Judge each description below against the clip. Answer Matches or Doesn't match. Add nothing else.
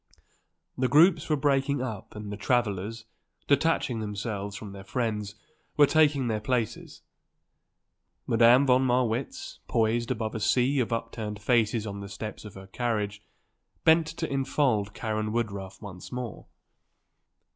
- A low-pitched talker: Matches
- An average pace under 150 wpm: Matches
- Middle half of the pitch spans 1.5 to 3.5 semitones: Doesn't match